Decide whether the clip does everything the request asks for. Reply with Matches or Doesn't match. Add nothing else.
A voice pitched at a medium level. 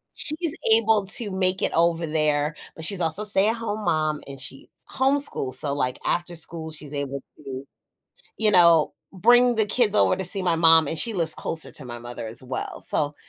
Matches